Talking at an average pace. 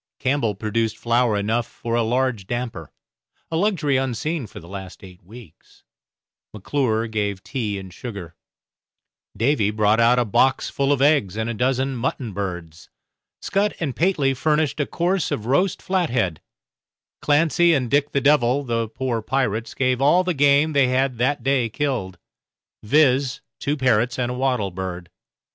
Yes: average, 155 wpm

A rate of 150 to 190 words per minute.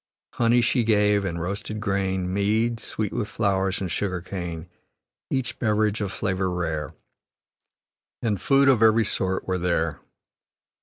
No: average, 140 wpm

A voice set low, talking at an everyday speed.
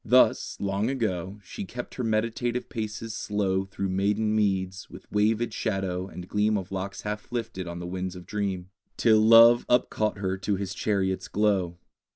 Yes: low, 100 Hz; average, 175 wpm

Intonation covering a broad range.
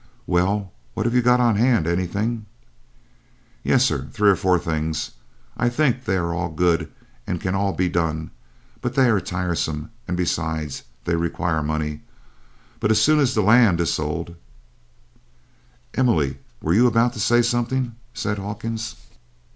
Yes: wide, 5.8 semitones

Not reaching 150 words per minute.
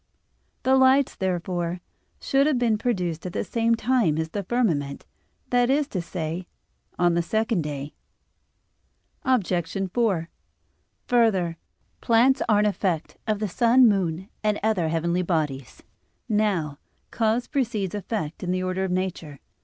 Yes: average, 140 wpm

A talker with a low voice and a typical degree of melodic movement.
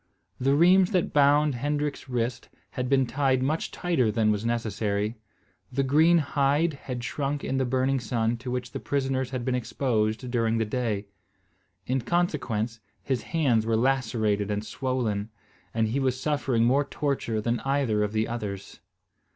Yes: low, 125 Hz; average, 3.6 semitones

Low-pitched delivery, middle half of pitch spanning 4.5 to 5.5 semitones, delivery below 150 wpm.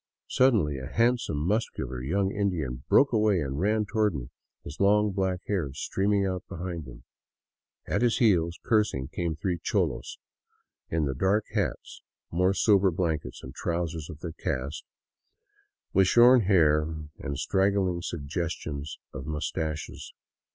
Yes: very low, 85 Hz; average, 5.0 semitones; slow, 135 wpm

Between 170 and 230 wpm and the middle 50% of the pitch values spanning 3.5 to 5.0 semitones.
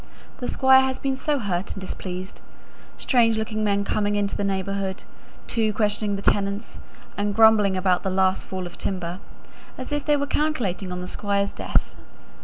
No: average, 175 wpm; average, 3.0 semitones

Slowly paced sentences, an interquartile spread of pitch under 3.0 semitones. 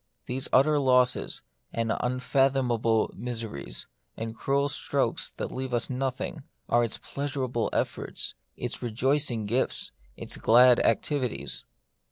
Yes: slow, 115 wpm; narrow, 2.6 semitones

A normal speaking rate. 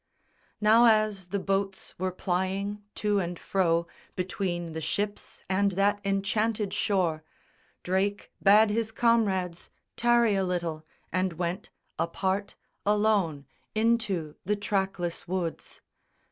No: slow, 115 wpm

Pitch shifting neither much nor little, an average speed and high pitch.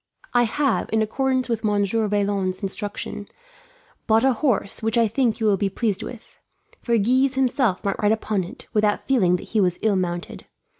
Yes: average, 3.3 semitones; average, 185 wpm; high, 215 Hz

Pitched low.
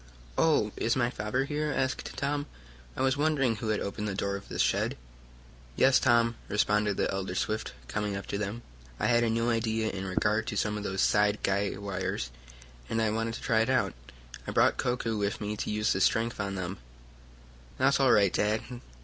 Yes: low, 110 Hz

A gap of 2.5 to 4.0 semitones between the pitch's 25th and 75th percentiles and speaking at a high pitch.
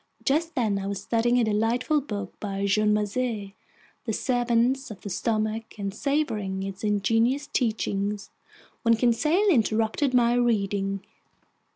Yes: average, 3.3 semitones; high, 225 Hz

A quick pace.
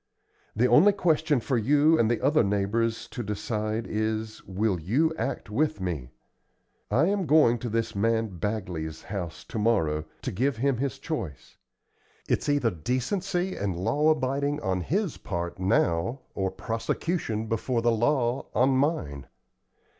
No: average, 145 wpm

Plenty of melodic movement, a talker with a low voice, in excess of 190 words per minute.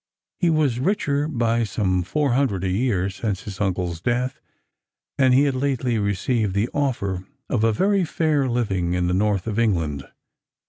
No: wide, 5.7 semitones; low, 115 Hz; average, 170 wpm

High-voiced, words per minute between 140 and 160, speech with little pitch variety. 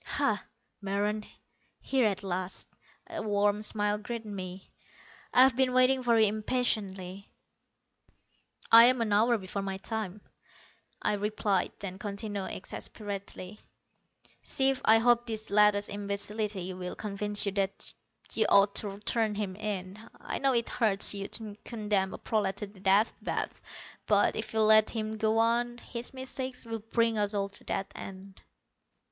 Yes: high, 210 Hz; average, 150 wpm; narrow, 2.3 semitones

